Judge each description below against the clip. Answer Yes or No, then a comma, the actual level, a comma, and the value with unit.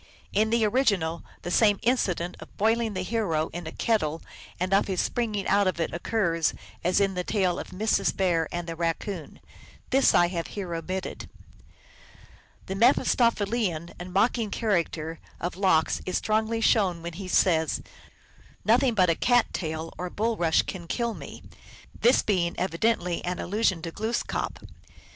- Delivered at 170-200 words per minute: No, average, 160 wpm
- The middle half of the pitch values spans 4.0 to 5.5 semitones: Yes, average, 4.3 semitones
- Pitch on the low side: No, medium, 185 Hz